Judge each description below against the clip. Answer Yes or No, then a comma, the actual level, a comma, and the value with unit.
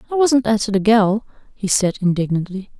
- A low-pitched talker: No, high, 210 Hz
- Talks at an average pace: Yes, average, 170 wpm